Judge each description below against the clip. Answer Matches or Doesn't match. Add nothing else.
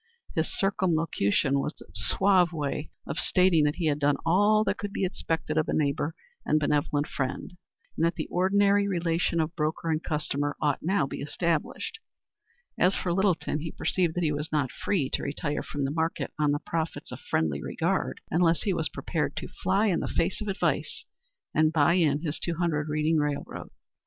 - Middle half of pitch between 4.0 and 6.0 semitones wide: Doesn't match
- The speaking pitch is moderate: Matches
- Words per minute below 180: Doesn't match